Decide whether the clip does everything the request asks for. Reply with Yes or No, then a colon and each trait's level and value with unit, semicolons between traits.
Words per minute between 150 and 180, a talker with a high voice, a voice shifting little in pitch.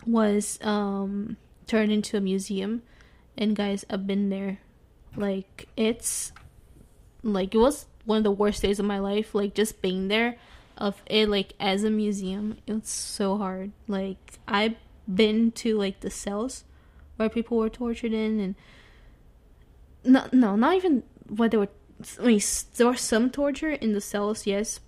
Yes: average, 160 wpm; high, 210 Hz; narrow, 2.0 semitones